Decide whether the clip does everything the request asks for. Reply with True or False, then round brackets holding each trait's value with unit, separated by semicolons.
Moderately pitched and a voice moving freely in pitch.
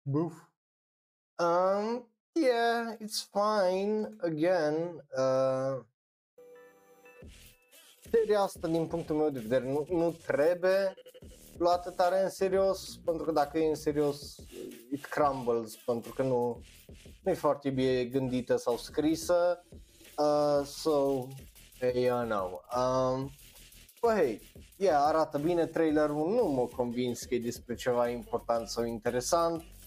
True (155 Hz; 5.8 semitones)